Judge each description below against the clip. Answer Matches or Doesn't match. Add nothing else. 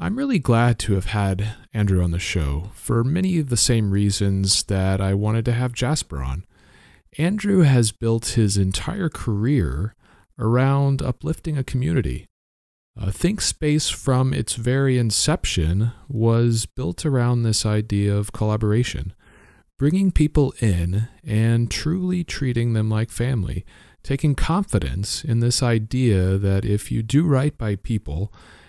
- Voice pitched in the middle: Doesn't match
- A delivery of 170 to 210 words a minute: Doesn't match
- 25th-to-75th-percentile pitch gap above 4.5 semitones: Matches